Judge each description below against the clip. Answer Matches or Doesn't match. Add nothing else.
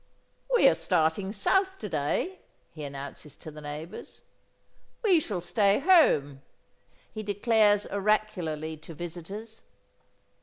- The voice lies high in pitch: Matches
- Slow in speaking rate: Matches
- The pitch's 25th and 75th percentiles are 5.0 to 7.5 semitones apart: Matches